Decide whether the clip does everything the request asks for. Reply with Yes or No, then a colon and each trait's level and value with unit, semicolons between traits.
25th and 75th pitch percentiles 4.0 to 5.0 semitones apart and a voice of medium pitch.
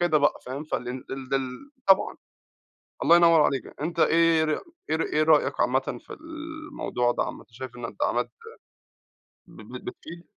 Yes: average, 4.6 semitones; medium, 155 Hz